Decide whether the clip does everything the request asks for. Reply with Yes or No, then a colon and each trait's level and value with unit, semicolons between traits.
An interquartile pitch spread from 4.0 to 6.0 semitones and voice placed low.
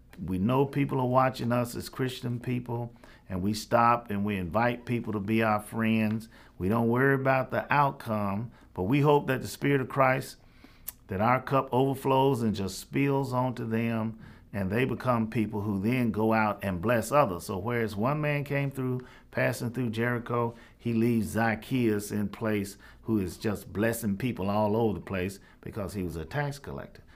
No: average, 3.2 semitones; low, 115 Hz